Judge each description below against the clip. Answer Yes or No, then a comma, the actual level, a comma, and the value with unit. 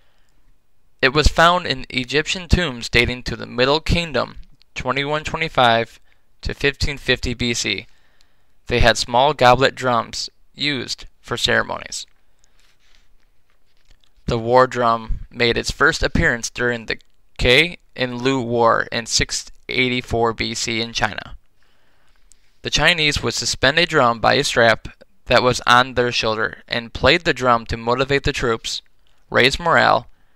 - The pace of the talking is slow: Yes, slow, 130 wpm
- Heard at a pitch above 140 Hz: No, low, 120 Hz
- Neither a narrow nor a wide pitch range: No, narrow, 2.0 semitones